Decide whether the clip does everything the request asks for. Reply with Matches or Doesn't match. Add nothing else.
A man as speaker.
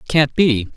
Matches